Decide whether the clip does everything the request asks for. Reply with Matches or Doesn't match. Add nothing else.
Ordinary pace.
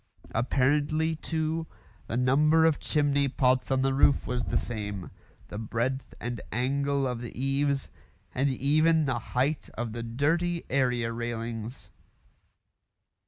Doesn't match